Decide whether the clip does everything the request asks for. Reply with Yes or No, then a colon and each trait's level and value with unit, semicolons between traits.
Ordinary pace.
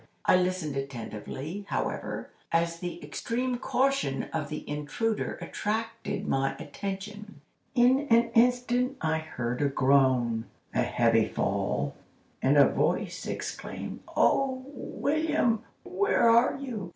No: slow, 115 wpm